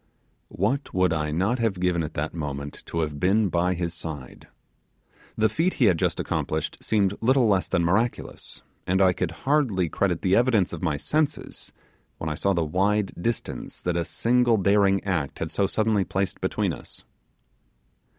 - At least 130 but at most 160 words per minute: No, average, 175 wpm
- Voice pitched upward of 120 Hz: No, very low, 95 Hz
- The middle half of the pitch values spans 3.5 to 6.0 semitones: Yes, average, 4.5 semitones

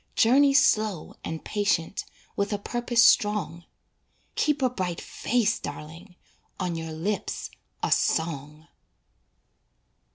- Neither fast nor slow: No, slow, 105 wpm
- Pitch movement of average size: No, wide, 5.7 semitones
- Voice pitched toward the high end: Yes, high, 200 Hz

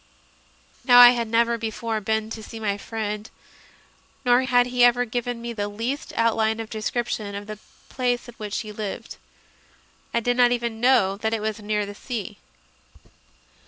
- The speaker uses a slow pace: No, average, 180 wpm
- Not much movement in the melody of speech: Yes, narrow, 2.3 semitones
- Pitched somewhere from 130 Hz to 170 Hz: No, high, 225 Hz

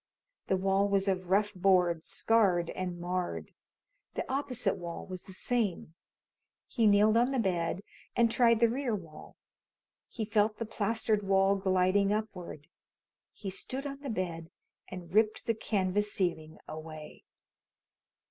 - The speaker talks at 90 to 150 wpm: Yes, average, 140 wpm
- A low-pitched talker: No, high, 195 Hz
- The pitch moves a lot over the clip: No, average, 3.4 semitones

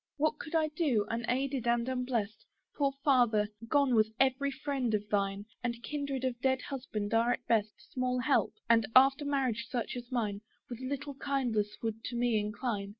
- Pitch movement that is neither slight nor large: Yes, average, 3.5 semitones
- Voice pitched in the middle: No, high, 245 Hz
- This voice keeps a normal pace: Yes, average, 175 wpm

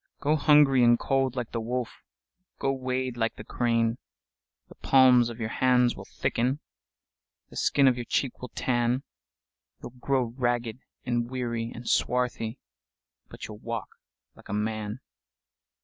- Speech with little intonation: Yes, narrow, 2.1 semitones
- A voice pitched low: Yes, low, 120 Hz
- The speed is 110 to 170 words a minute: Yes, slow, 135 wpm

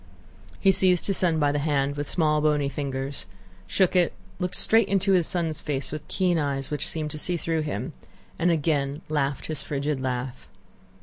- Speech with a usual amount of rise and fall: Yes, average, 3.5 semitones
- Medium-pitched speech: Yes, medium, 150 Hz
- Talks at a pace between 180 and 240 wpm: Yes, average, 185 wpm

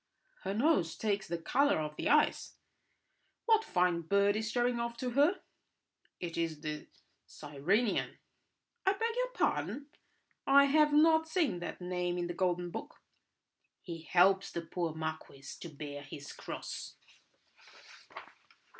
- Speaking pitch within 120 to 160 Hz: No, medium, 185 Hz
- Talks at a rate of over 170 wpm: No, slow, 135 wpm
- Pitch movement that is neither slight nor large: No, wide, 8.9 semitones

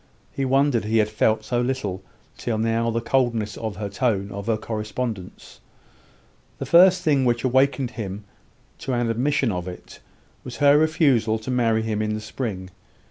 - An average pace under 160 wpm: No, average, 170 wpm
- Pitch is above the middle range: No, low, 115 Hz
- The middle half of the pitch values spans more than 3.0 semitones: Yes, average, 3.4 semitones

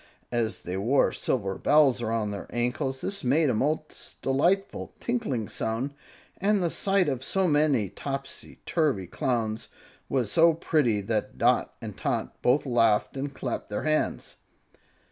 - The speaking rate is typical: Yes, average, 145 wpm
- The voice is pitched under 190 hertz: Yes, low, 135 Hz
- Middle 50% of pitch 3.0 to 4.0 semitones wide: No, average, 5.3 semitones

